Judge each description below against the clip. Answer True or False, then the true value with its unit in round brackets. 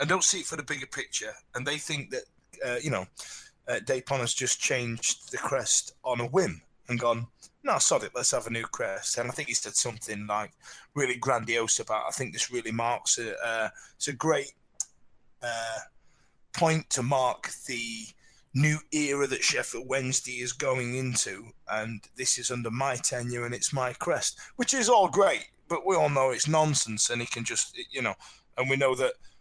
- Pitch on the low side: True (125 Hz)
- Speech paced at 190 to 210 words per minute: True (200 wpm)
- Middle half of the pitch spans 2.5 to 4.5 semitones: True (3.2 semitones)